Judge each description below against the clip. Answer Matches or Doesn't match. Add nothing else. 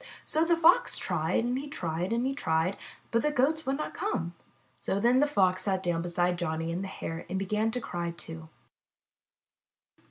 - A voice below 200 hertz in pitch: Matches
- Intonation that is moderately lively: Doesn't match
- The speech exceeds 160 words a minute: Matches